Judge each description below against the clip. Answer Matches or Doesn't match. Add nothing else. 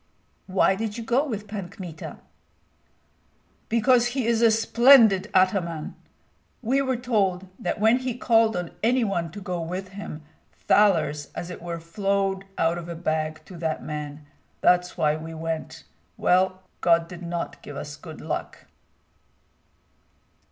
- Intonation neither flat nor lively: Matches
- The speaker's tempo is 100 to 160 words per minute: Matches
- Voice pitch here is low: Doesn't match